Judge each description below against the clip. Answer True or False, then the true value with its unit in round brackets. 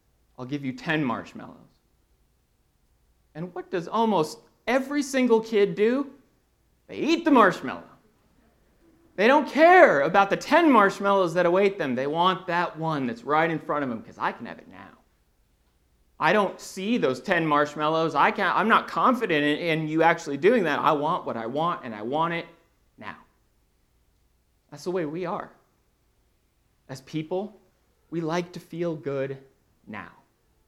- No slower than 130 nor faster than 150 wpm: False (160 wpm)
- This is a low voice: False (170 Hz)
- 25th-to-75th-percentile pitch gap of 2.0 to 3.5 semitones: False (5.4 semitones)